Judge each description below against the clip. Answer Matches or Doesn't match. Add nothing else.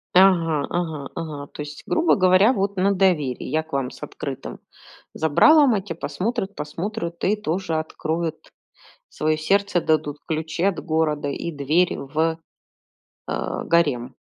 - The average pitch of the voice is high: Doesn't match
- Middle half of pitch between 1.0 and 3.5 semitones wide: Doesn't match